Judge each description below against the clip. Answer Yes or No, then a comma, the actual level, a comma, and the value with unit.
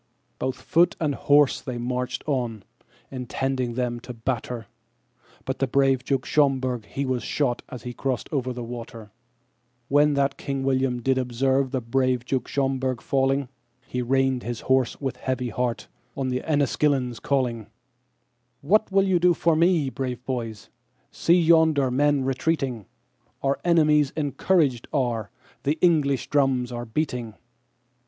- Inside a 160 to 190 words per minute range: No, slow, 135 wpm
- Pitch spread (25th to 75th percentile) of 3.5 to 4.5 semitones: No, narrow, 2.4 semitones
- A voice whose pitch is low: Yes, low, 130 Hz